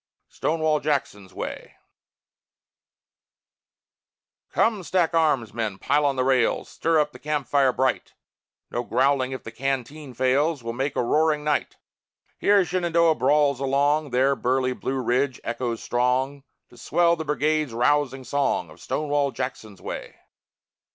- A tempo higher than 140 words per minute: No, slow, 135 wpm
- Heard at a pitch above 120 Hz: Yes, medium, 140 Hz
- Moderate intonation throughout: Yes, average, 3.1 semitones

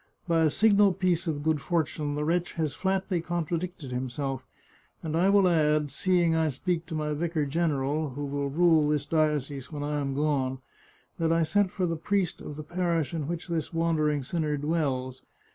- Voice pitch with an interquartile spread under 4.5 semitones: Yes, average, 2.9 semitones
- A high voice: No, medium, 160 Hz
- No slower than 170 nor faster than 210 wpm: Yes, average, 190 wpm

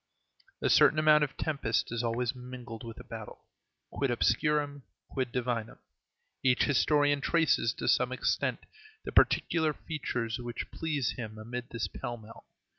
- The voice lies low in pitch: Yes, low, 125 Hz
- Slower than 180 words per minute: Yes, average, 145 wpm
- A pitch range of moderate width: Yes, average, 3.9 semitones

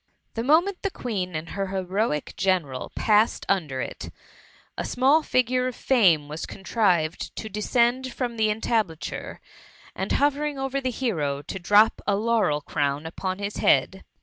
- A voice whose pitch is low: No, high, 210 Hz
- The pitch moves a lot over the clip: Yes, wide, 6.6 semitones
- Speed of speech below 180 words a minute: Yes, average, 155 wpm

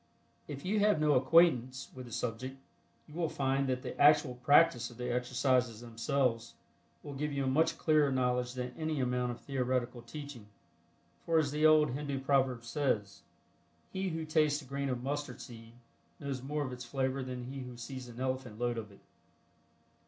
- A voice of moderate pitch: No, low, 130 Hz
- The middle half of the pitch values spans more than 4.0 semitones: No, average, 2.9 semitones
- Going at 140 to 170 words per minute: No, average, 180 wpm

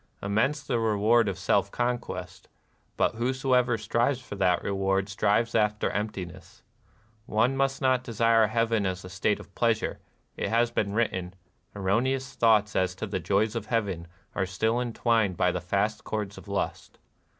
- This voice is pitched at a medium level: No, low, 110 Hz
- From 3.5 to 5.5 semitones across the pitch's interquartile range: No, average, 3.1 semitones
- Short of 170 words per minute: Yes, average, 160 wpm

